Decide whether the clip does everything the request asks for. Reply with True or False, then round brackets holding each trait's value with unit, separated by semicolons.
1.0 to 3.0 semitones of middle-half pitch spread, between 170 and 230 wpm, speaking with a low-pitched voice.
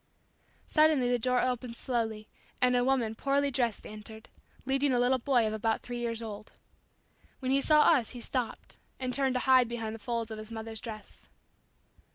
False (2.7 semitones; 185 wpm; 245 Hz)